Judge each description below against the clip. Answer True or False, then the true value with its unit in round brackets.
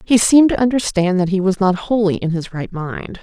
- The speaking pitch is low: False (195 Hz)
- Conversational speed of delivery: False (240 wpm)